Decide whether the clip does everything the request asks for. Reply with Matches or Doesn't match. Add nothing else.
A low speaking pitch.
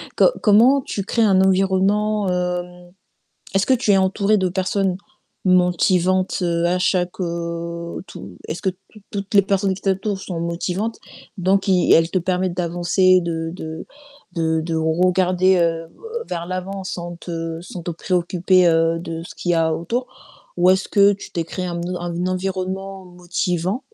Doesn't match